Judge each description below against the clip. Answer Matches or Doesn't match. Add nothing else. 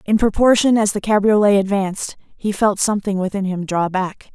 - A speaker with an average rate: Matches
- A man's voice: Doesn't match